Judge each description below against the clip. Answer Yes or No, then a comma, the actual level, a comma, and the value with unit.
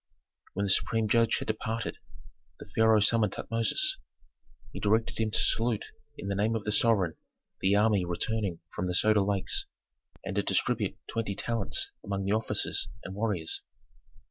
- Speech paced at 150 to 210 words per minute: Yes, average, 160 wpm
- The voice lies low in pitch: Yes, low, 105 Hz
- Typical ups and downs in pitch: No, narrow, 2.3 semitones